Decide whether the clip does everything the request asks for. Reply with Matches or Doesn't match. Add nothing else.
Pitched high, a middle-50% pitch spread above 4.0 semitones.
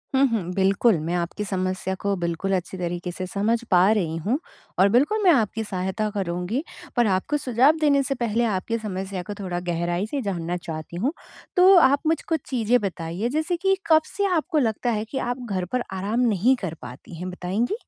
Matches